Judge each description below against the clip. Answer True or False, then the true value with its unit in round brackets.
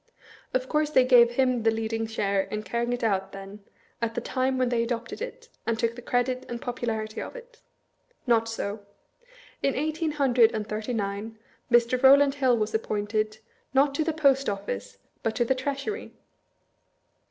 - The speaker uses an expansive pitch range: False (3.4 semitones)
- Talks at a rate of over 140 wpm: True (180 wpm)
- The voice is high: True (240 Hz)